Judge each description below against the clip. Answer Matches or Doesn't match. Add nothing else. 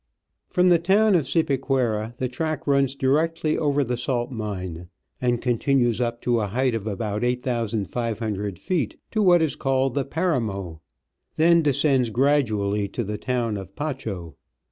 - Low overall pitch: Matches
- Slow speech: Doesn't match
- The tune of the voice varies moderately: Matches